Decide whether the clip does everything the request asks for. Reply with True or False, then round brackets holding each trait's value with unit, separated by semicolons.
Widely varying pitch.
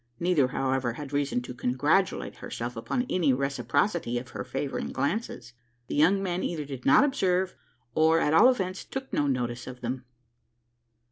True (6.4 semitones)